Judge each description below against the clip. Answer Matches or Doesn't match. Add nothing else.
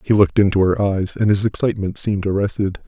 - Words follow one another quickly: Matches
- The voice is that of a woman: Doesn't match